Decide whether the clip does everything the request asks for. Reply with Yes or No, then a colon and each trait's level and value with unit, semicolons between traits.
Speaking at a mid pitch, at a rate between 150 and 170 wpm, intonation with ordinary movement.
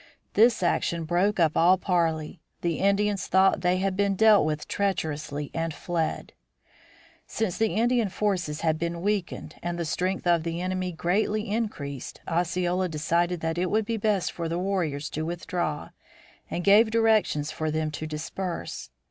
Yes: medium, 175 Hz; average, 160 wpm; average, 3.6 semitones